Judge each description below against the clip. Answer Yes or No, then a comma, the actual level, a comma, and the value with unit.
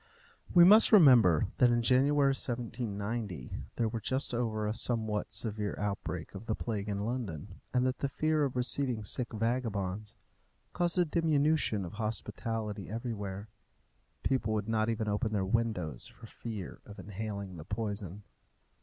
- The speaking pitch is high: No, low, 110 Hz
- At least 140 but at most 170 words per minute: Yes, average, 150 wpm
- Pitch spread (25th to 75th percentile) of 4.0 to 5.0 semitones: No, average, 3.5 semitones